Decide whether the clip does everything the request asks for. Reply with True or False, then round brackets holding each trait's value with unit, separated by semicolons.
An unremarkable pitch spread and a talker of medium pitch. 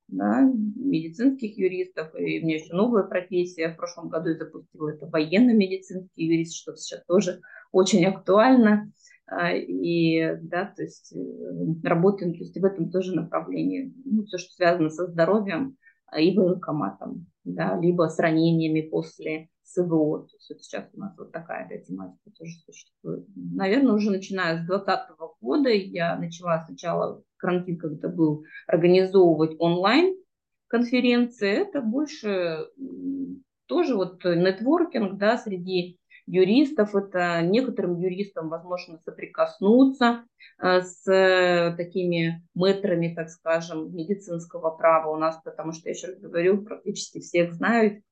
True (4.3 semitones; 180 Hz)